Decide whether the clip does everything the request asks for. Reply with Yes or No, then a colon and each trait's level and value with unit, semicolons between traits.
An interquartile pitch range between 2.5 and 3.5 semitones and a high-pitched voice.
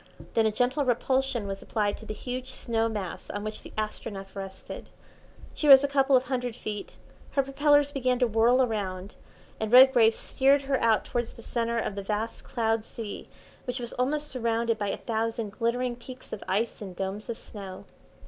Yes: average, 3.2 semitones; high, 230 Hz